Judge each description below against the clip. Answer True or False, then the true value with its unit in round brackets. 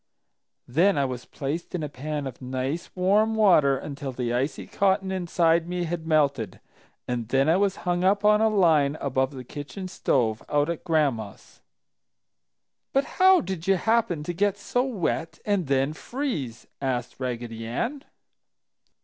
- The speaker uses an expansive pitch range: True (6.3 semitones)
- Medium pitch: True (160 Hz)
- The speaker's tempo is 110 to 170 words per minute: True (160 wpm)